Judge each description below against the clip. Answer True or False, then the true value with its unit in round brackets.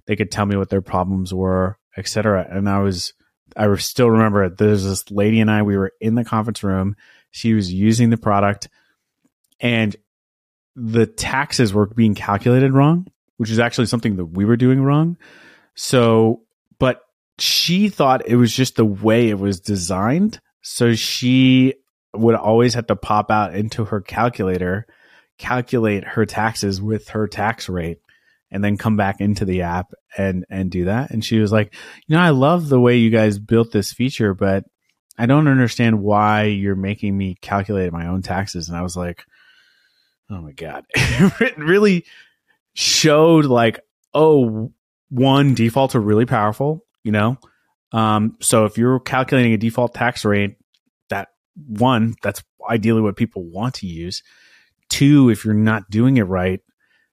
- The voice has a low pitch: True (110 Hz)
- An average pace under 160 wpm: False (165 wpm)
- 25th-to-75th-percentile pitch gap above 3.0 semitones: True (3.9 semitones)